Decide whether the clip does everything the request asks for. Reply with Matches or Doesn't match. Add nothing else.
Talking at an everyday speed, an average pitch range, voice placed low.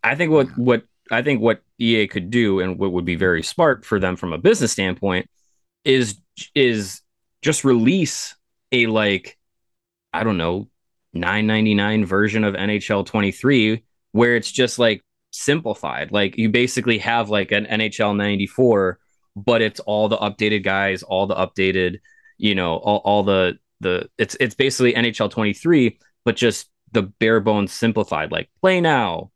Matches